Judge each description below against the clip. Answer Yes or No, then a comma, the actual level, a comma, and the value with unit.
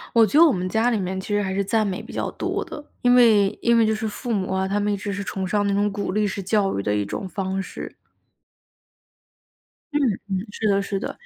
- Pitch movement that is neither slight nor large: No, narrow, 2.3 semitones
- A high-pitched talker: Yes, high, 200 Hz